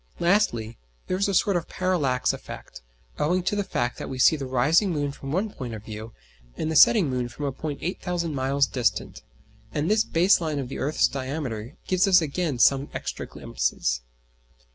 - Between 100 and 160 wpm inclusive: No, average, 190 wpm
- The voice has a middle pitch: Yes, medium, 145 Hz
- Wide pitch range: Yes, wide, 5.8 semitones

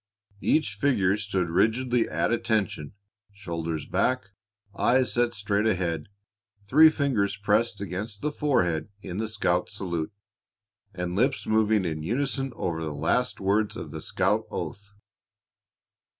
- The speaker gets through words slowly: Yes, slow, 130 wpm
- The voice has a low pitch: Yes, low, 105 Hz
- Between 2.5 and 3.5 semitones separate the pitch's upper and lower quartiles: No, average, 5.1 semitones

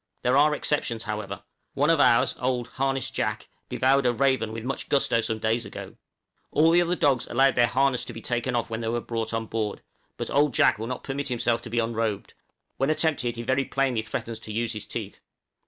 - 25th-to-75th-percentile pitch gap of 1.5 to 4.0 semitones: Yes, average, 3.2 semitones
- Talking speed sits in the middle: No, fast, 215 wpm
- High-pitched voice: No, low, 120 Hz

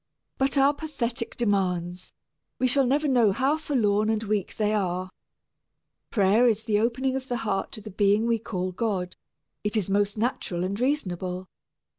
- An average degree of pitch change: Yes, average, 4.3 semitones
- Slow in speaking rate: No, average, 165 wpm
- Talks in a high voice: Yes, high, 215 Hz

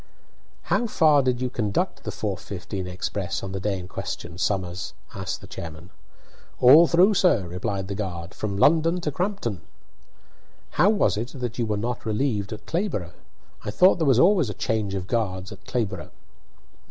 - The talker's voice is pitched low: Yes, low, 105 Hz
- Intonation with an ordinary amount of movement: No, wide, 6.8 semitones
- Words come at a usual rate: Yes, average, 170 wpm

